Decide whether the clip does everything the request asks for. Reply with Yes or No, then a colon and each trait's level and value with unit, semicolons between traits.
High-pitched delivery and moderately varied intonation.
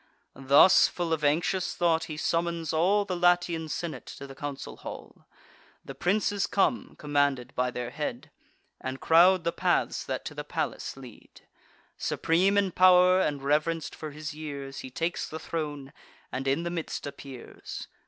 No: medium, 160 Hz; average, 3.8 semitones